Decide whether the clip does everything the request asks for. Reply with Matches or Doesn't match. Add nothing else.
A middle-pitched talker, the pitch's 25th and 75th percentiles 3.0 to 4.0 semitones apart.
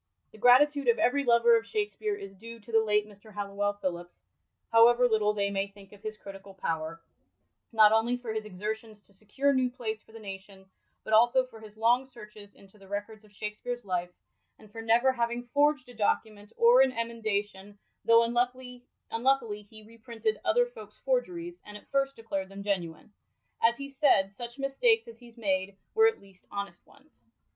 Doesn't match